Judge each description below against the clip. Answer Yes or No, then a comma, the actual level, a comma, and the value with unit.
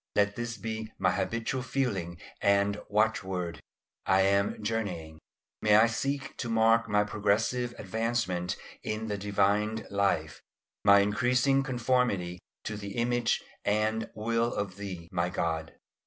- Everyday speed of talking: No, slow, 130 wpm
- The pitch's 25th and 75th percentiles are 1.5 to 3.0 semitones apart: Yes, average, 2.7 semitones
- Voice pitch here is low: Yes, low, 105 Hz